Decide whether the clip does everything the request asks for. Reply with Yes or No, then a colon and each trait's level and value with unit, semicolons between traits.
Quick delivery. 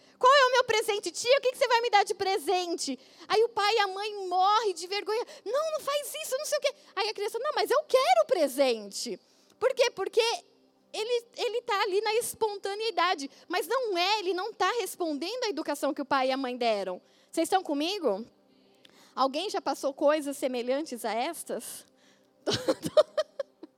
Yes: fast, 190 wpm